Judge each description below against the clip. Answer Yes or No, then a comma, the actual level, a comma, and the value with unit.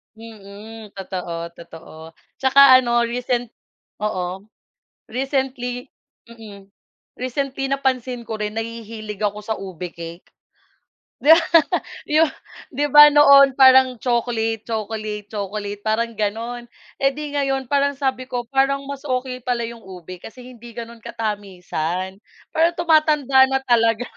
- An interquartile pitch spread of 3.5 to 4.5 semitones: Yes, average, 4.1 semitones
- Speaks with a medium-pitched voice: No, high, 235 Hz